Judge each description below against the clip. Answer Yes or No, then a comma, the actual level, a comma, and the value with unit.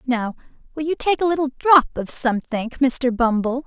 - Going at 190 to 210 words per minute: No, average, 180 wpm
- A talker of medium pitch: No, very high, 265 Hz